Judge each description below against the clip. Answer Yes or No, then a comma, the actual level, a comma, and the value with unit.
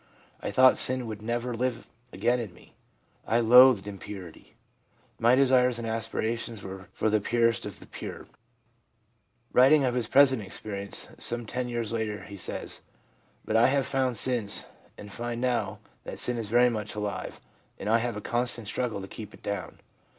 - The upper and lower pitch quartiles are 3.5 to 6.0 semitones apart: No, average, 2.9 semitones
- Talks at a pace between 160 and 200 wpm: Yes, average, 175 wpm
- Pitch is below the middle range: Yes, low, 115 Hz